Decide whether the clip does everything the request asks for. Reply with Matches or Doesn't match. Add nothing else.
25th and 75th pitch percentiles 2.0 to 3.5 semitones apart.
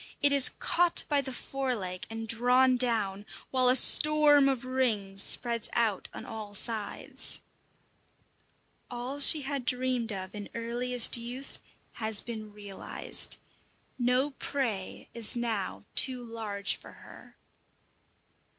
Matches